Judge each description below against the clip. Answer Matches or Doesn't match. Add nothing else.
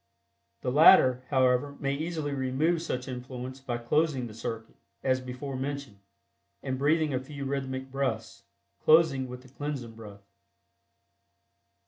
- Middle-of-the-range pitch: Doesn't match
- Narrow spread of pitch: Matches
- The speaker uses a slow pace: Matches